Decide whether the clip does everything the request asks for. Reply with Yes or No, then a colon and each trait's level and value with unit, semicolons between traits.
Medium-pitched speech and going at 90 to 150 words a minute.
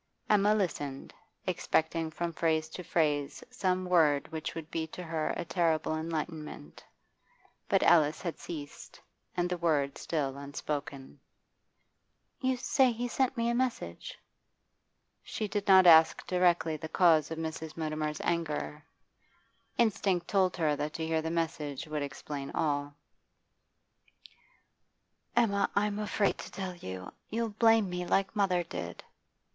Yes: medium, 165 Hz; average, 140 wpm